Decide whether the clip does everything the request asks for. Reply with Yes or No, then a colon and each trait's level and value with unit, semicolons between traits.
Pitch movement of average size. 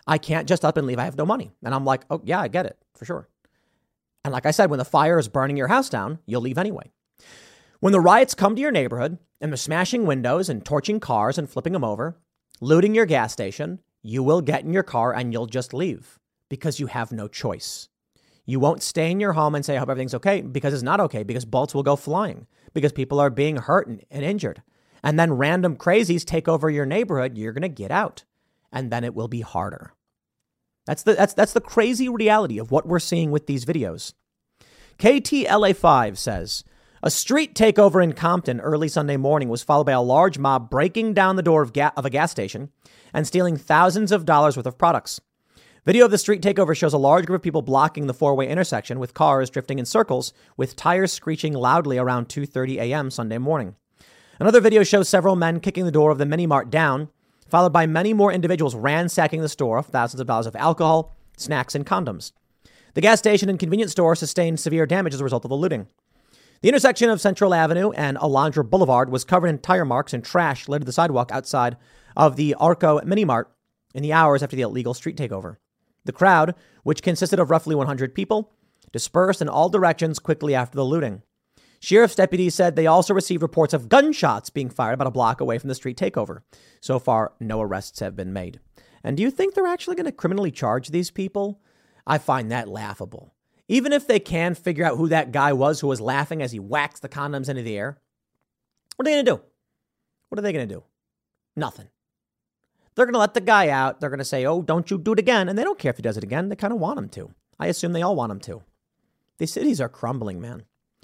No: wide, 5.9 semitones